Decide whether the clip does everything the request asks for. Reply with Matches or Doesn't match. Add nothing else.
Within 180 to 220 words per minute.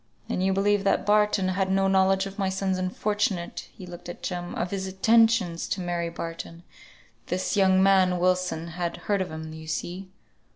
Matches